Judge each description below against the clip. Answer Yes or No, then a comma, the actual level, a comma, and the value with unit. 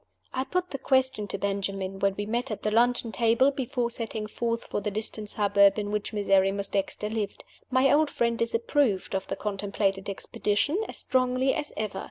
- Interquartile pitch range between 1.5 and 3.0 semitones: No, average, 3.9 semitones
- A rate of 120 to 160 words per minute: No, average, 185 wpm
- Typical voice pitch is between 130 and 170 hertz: No, high, 215 Hz